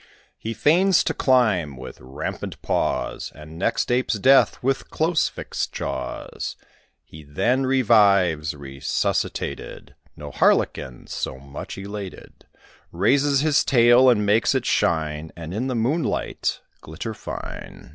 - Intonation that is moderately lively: No, wide, 8.8 semitones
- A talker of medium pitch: No, low, 105 Hz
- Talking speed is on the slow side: Yes, slow, 125 wpm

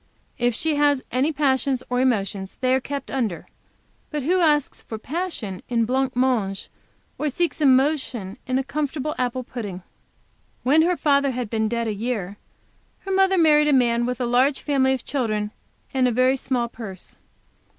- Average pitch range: Yes, average, 3.7 semitones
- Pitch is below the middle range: No, very high, 255 Hz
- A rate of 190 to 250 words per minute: No, average, 170 wpm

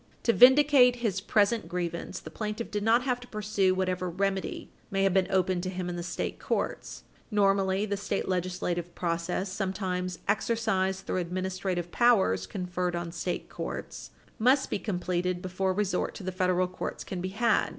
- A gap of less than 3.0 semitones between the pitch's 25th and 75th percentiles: Yes, narrow, 2.6 semitones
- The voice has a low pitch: No, high, 190 Hz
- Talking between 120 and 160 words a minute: No, average, 170 wpm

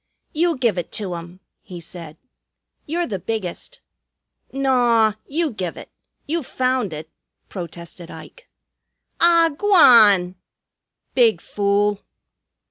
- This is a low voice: No, high, 215 Hz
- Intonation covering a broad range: Yes, wide, 7.5 semitones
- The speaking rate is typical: No, slow, 110 wpm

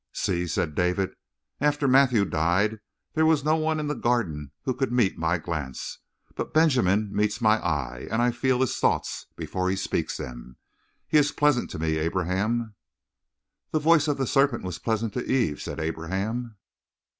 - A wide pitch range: Yes, wide, 7.4 semitones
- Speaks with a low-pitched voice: Yes, low, 110 Hz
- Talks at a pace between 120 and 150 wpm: No, average, 170 wpm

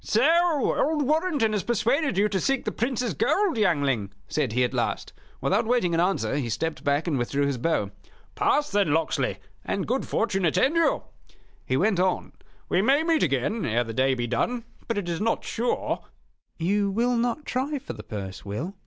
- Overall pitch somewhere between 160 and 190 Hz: No, high, 200 Hz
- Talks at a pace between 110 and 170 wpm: No, average, 195 wpm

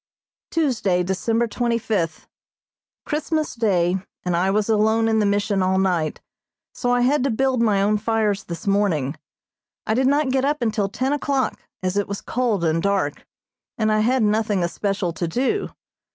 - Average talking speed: Yes, average, 170 wpm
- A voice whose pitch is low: No, high, 215 Hz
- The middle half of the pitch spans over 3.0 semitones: Yes, average, 4.4 semitones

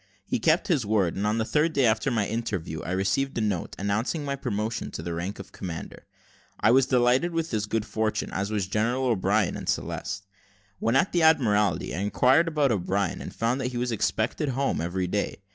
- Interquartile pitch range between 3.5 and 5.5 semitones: Yes, average, 4.8 semitones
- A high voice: No, low, 110 Hz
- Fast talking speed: Yes, fast, 210 wpm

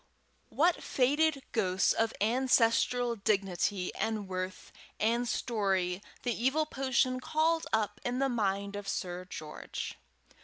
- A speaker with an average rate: No, slow, 120 wpm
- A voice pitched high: Yes, high, 225 Hz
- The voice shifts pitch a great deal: No, average, 4.8 semitones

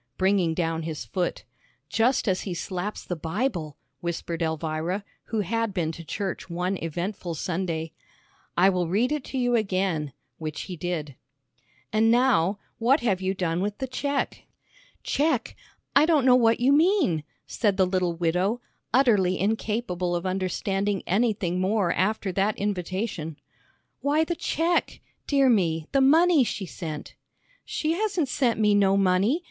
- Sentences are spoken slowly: No, average, 150 wpm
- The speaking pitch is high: Yes, high, 195 Hz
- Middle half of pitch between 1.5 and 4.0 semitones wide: No, average, 5.3 semitones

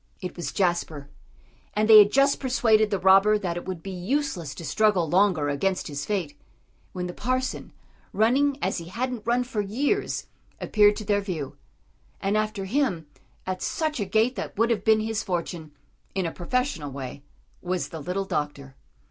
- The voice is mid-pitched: No, high, 195 Hz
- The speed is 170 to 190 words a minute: Yes, average, 175 wpm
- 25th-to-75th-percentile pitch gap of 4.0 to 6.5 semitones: Yes, average, 4.3 semitones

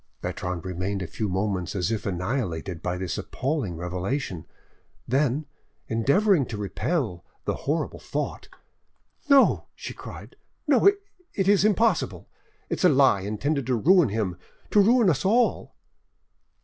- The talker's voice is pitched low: Yes, low, 125 Hz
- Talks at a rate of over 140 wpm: No, slow, 135 wpm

